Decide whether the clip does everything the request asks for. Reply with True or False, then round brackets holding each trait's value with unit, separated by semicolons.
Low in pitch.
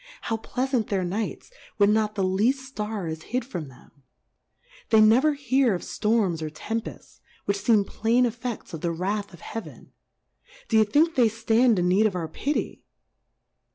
False (215 Hz)